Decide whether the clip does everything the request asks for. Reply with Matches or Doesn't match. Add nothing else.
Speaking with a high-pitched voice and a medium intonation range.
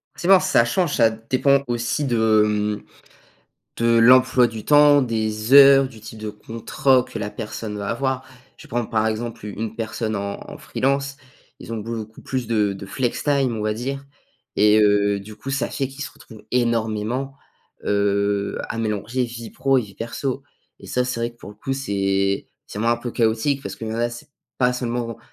Doesn't match